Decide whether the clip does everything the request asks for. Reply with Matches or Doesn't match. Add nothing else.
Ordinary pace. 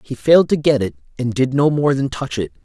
Doesn't match